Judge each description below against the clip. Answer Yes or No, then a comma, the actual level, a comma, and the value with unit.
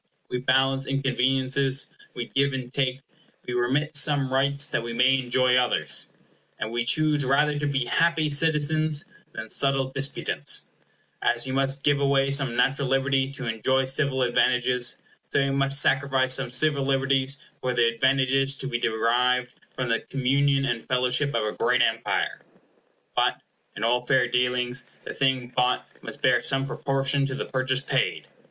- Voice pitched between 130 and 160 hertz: Yes, low, 135 Hz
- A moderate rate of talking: Yes, average, 160 wpm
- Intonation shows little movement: Yes, narrow, 1.7 semitones